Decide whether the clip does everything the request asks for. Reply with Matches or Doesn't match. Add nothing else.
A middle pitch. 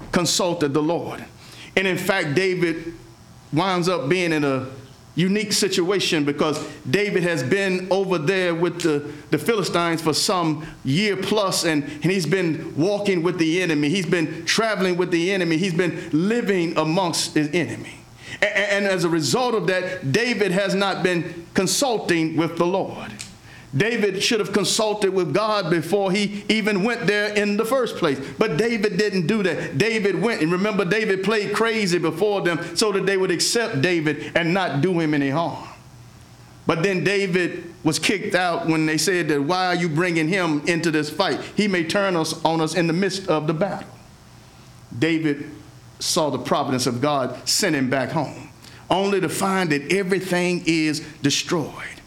Matches